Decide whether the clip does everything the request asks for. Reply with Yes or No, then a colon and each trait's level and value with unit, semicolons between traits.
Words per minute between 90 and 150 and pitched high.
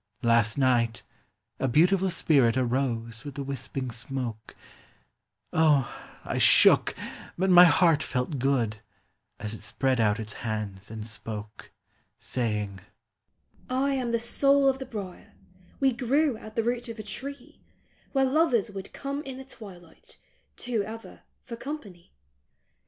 No: average, 140 wpm; medium, 160 Hz